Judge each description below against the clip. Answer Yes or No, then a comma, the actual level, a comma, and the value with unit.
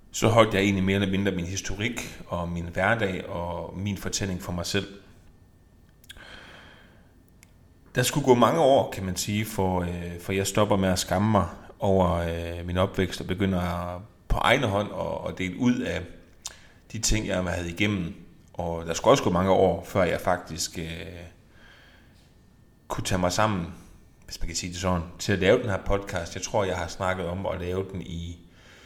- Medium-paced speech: Yes, average, 185 wpm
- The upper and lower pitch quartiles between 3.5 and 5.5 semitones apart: No, narrow, 2.4 semitones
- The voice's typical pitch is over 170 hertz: No, very low, 90 Hz